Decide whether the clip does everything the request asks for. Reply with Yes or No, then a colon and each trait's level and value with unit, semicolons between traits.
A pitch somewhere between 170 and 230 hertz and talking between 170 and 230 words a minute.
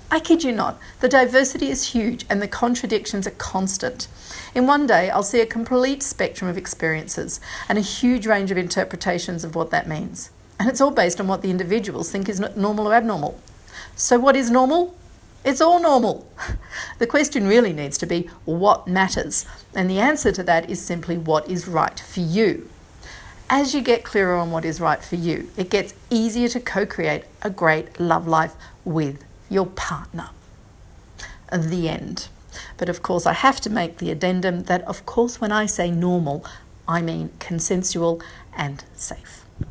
Yes: high, 190 Hz; average, 180 wpm